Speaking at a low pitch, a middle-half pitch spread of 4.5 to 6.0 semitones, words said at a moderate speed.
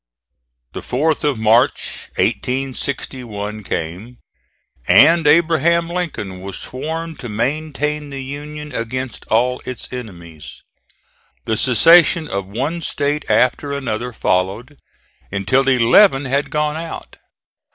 No: low, 130 Hz; average, 5.1 semitones; slow, 110 wpm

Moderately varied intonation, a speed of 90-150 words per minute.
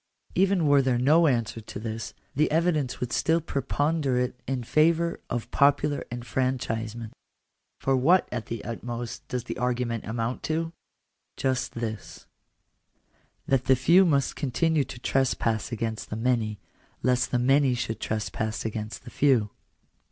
Yes: average, 3.9 semitones; average, 145 wpm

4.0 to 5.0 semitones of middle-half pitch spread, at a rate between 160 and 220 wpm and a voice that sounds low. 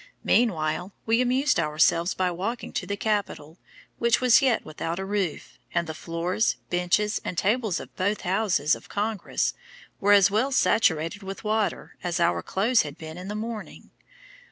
No: average, 4.4 semitones; average, 165 wpm; high, 195 Hz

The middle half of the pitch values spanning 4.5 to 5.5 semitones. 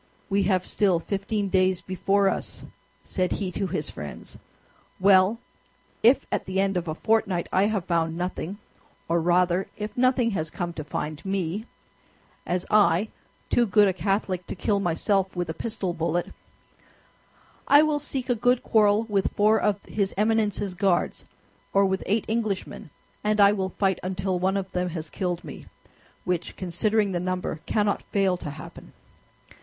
No: average, 2.8 semitones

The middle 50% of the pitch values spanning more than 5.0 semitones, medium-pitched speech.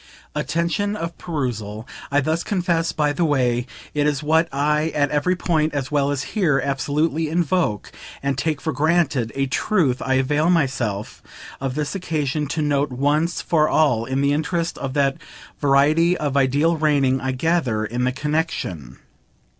No: average, 3.4 semitones; medium, 145 Hz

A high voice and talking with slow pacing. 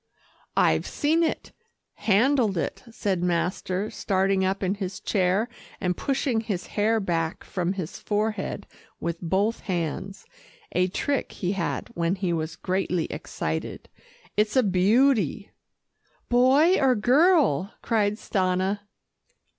Yes: high, 195 Hz; slow, 125 wpm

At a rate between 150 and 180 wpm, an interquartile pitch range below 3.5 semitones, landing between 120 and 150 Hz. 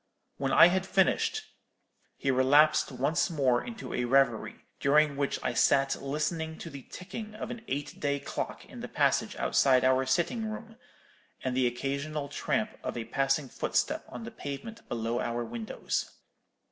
No: average, 160 wpm; average, 4.3 semitones; medium, 140 Hz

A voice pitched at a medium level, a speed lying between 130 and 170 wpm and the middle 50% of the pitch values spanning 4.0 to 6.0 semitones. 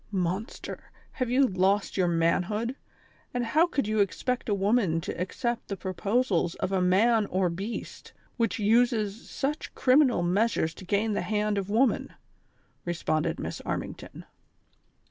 No: high, 205 Hz; average, 145 wpm; average, 4.3 semitones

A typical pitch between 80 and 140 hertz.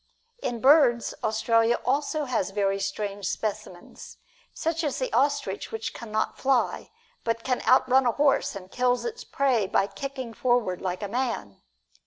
No: high, 235 Hz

